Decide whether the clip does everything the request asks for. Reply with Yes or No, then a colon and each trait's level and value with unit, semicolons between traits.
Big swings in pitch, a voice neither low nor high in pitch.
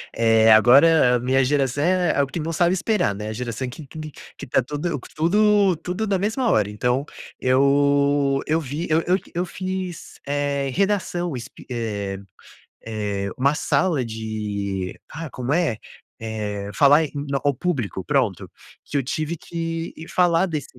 Yes: wide, 6.3 semitones; medium, 145 Hz